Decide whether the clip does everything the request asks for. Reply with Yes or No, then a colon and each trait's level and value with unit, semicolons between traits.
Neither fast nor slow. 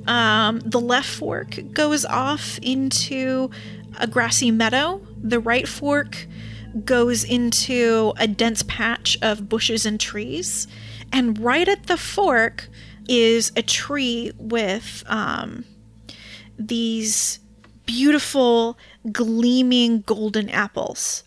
No: slow, 105 wpm